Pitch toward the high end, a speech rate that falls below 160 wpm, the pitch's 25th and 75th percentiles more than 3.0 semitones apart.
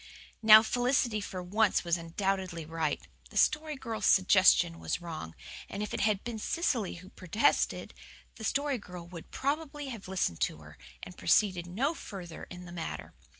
No: high, 195 Hz; average, 165 wpm; average, 5.0 semitones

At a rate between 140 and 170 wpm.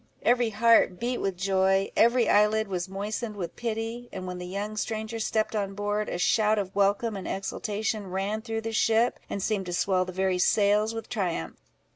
No: average, 190 wpm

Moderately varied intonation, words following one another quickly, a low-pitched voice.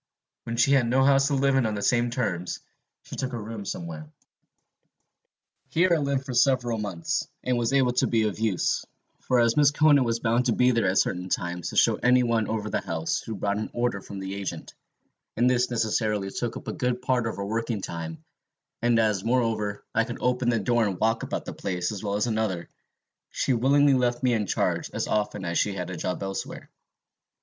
Yes: average, 3.8 semitones; fast, 215 wpm; low, 115 Hz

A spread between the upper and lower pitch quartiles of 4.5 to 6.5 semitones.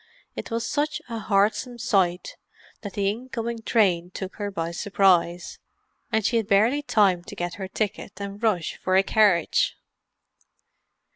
No: average, 3.4 semitones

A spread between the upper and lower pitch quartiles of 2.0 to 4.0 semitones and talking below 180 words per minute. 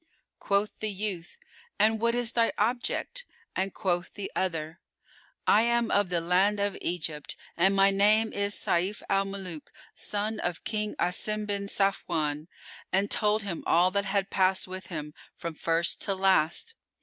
Yes: average, 3.1 semitones; average, 160 wpm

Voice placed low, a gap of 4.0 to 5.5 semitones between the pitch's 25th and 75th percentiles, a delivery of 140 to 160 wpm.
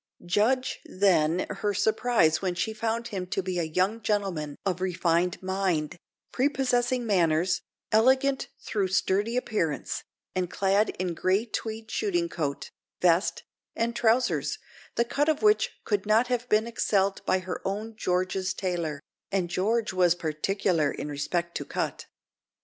No: high, 195 Hz; average, 4.4 semitones; average, 145 wpm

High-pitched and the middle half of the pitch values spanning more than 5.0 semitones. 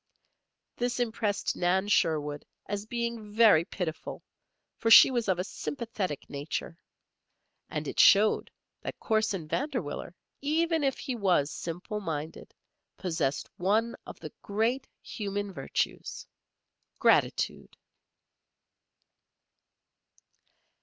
Yes: high, 205 Hz; wide, 5.4 semitones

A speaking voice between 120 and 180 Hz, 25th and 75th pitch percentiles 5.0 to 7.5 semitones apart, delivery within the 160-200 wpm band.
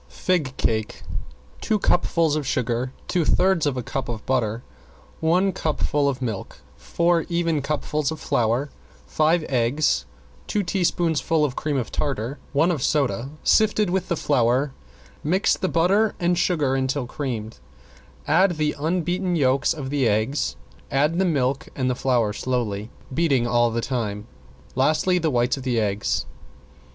No: medium, 140 Hz; wide, 5.4 semitones; average, 150 wpm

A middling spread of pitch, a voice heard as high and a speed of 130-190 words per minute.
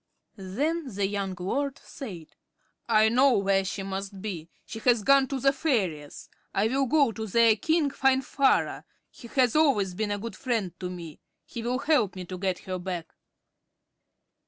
No: wide, 5.8 semitones; high, 220 Hz; average, 170 wpm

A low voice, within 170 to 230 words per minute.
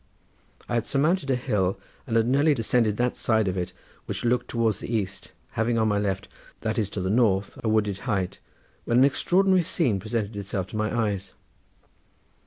Yes: low, 110 Hz; average, 190 wpm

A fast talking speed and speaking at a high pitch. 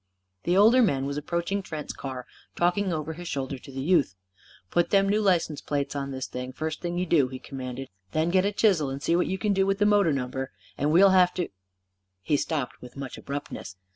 No: fast, 220 wpm; medium, 155 Hz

